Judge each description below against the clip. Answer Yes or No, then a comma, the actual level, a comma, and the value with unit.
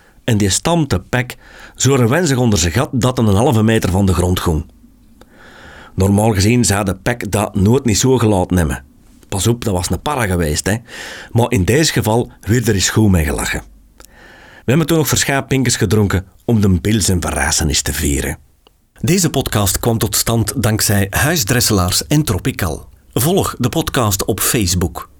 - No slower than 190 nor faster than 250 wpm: No, average, 175 wpm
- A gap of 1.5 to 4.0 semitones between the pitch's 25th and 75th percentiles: No, average, 4.9 semitones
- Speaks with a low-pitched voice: Yes, low, 105 Hz